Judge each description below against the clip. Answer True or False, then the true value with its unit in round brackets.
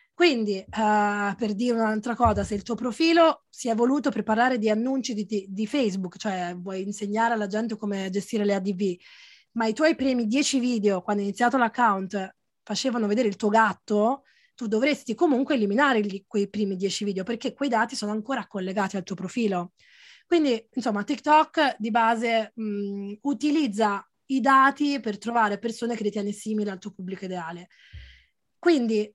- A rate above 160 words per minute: True (170 wpm)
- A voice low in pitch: False (220 Hz)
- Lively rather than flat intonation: False (3.6 semitones)